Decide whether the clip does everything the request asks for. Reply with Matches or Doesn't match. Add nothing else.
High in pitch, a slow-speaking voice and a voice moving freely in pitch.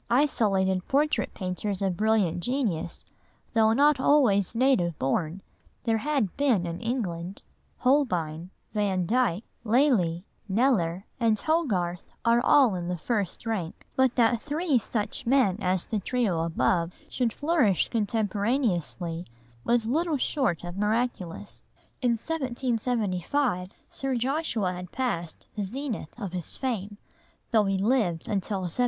Matches